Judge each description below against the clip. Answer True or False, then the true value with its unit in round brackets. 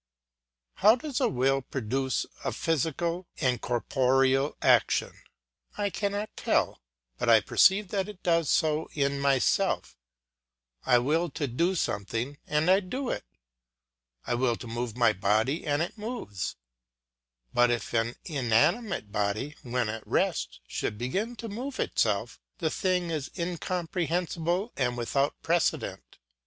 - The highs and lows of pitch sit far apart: True (6.8 semitones)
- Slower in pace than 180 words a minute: True (135 wpm)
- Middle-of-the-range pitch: True (145 Hz)